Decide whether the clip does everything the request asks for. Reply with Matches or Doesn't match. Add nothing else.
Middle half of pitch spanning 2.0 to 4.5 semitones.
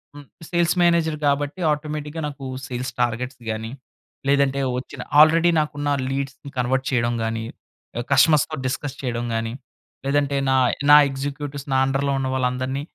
Matches